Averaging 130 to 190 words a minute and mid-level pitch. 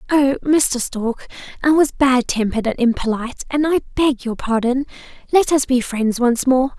No: average, 175 wpm; very high, 260 Hz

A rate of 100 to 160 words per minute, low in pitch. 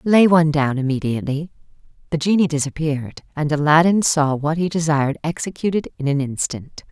No: average, 150 wpm; medium, 155 Hz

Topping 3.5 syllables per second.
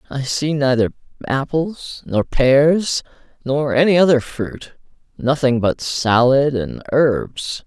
No: 3.4 syllables/s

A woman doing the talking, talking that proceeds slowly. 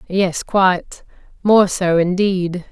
Yes: female; slow, 90 wpm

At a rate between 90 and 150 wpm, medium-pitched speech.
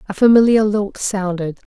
No: average, 140 wpm; high, 200 Hz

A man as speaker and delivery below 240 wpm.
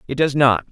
No: male; fast, 255 wpm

